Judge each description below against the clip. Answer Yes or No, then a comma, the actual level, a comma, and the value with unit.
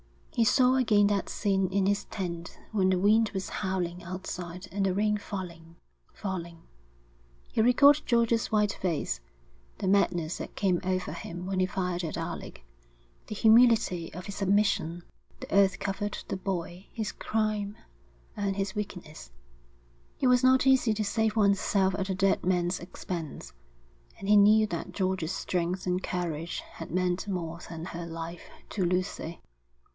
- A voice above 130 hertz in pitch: Yes, high, 190 Hz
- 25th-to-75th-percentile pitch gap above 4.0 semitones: No, average, 2.9 semitones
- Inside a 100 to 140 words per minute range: No, average, 160 wpm